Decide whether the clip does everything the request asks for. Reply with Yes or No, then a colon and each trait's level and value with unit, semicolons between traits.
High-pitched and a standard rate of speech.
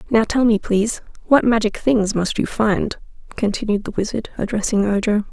Yes: high, 215 Hz; average, 170 wpm